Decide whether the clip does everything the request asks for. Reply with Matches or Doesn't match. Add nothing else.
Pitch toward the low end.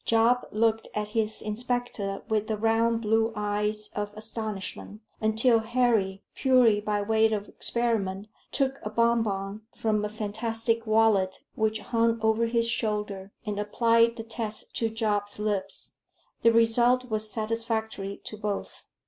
Doesn't match